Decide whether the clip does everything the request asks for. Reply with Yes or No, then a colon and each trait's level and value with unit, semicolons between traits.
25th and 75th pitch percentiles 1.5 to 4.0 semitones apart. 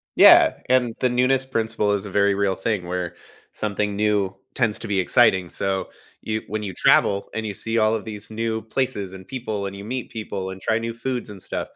Yes: narrow, 2.6 semitones